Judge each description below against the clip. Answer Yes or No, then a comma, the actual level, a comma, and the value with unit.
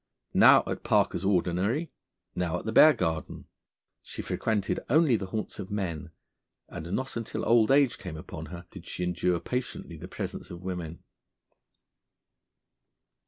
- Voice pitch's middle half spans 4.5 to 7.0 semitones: Yes, average, 5.0 semitones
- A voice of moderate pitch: No, very low, 95 Hz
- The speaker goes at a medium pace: Yes, average, 145 wpm